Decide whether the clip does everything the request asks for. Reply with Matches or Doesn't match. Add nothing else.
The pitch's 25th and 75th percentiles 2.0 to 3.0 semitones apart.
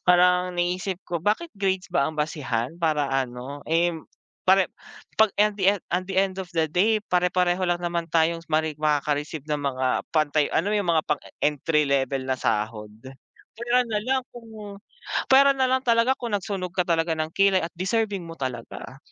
Doesn't match